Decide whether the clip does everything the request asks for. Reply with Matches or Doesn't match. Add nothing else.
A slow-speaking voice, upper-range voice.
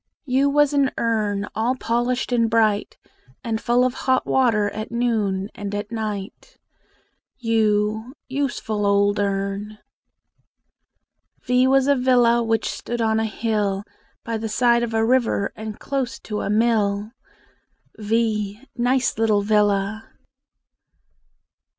Matches